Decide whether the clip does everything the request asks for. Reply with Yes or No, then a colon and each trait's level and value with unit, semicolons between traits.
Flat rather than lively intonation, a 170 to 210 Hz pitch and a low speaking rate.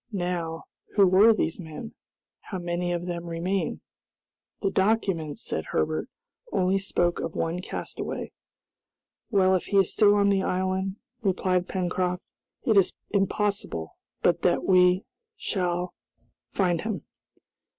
Yes: narrow, 2.0 semitones; medium, 185 Hz; slow, 130 wpm